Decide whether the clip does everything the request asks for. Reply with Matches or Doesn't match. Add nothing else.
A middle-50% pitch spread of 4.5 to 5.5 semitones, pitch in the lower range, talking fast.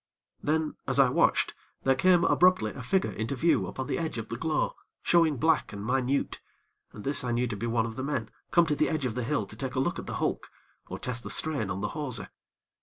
Matches